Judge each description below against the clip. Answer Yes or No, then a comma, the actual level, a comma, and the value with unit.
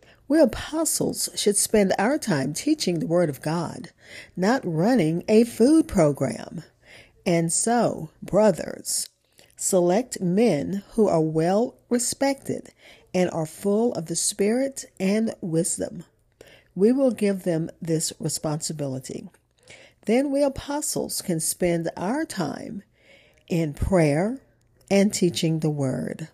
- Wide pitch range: Yes, wide, 5.9 semitones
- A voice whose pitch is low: No, high, 190 Hz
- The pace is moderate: No, slow, 120 wpm